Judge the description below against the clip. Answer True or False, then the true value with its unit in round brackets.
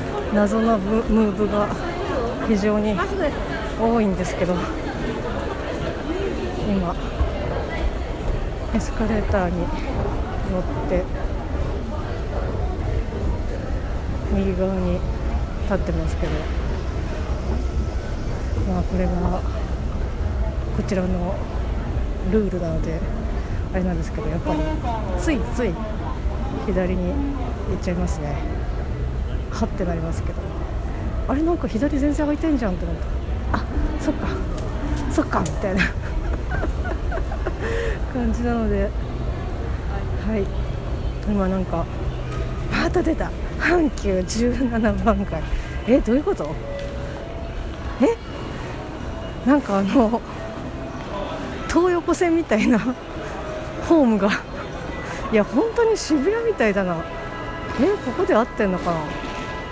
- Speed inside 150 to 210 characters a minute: True (190 characters per minute)